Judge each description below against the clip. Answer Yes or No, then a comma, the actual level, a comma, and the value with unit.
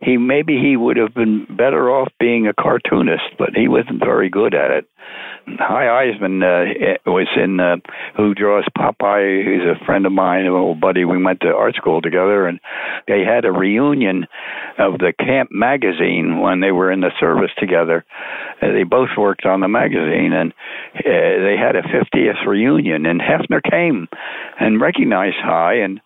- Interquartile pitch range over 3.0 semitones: No, narrow, 2.5 semitones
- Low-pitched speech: Yes, very low, 95 Hz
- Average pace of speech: Yes, average, 180 wpm